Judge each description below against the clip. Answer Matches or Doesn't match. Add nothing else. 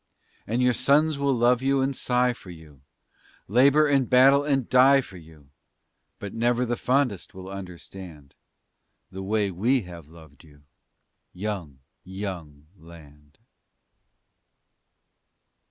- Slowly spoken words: Matches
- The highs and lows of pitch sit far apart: Matches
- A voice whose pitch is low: Matches